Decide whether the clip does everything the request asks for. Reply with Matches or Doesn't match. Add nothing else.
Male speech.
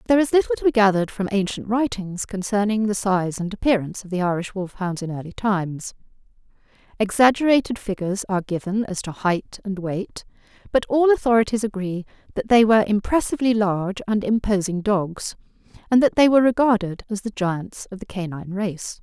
Doesn't match